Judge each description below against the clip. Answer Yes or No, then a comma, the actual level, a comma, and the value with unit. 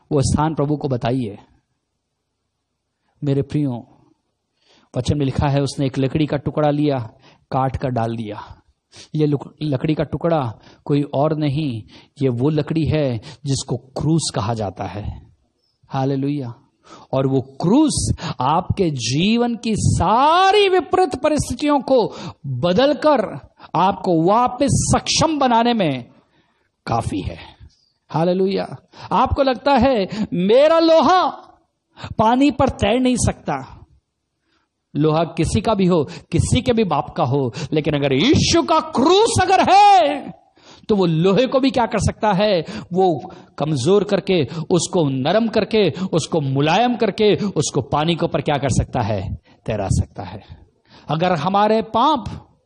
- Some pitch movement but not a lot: No, wide, 8.5 semitones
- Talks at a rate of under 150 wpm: Yes, slow, 135 wpm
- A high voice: No, medium, 155 Hz